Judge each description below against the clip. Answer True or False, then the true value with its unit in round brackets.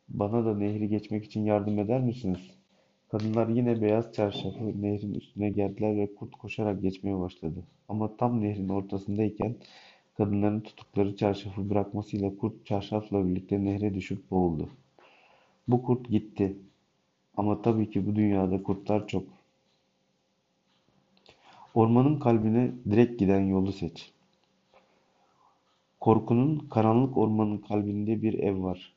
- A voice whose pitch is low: True (105 Hz)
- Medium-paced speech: True (120 wpm)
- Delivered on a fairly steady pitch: True (1.9 semitones)